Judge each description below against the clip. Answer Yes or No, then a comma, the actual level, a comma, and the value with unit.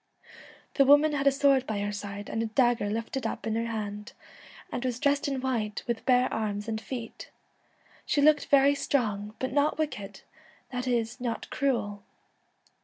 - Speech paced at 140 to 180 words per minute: Yes, average, 175 wpm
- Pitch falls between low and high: No, high, 240 Hz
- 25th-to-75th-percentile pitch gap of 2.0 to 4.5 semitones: Yes, average, 4.2 semitones